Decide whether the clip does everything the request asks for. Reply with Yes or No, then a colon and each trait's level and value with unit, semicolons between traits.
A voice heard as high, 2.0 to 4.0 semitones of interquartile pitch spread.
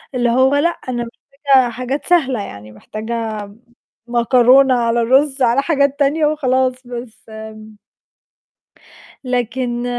Yes: very high, 250 Hz; average, 2.8 semitones